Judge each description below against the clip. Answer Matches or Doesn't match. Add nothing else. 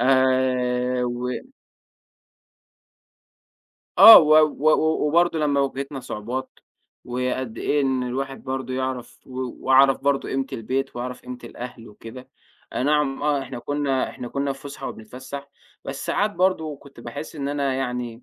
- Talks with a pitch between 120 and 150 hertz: Matches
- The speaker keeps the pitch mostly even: Matches